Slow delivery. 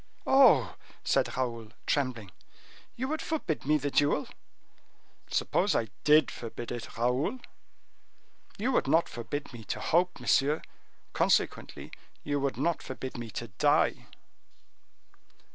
Yes: slow, 125 wpm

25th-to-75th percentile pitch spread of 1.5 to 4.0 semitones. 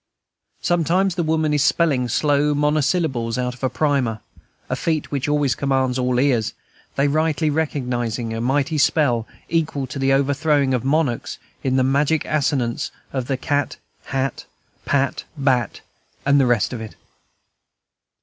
Yes: average, 3.0 semitones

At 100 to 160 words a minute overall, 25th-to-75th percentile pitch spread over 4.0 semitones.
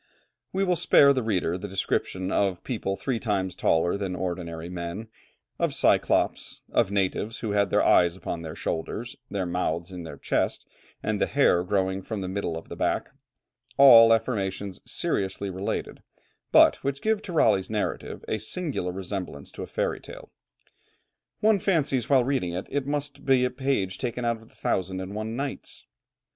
No: average, 175 wpm; wide, 5.5 semitones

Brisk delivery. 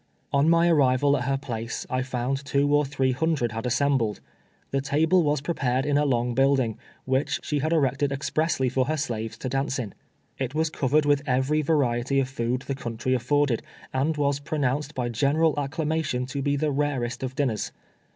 No: average, 190 wpm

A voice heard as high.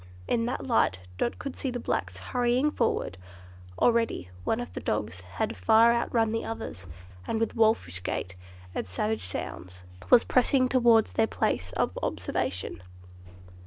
Yes: high, 225 Hz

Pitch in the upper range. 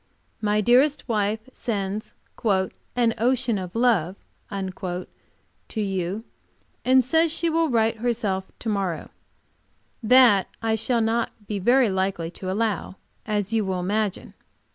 Yes: high, 215 Hz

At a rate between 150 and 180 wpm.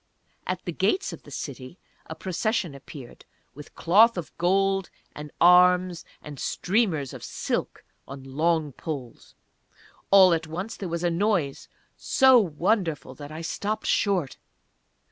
No: average, 140 wpm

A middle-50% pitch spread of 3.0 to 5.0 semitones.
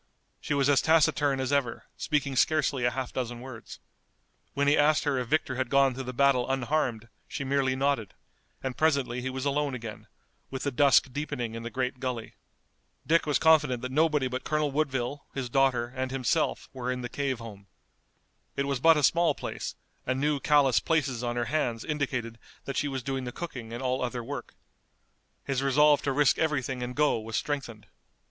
No: narrow, 2.6 semitones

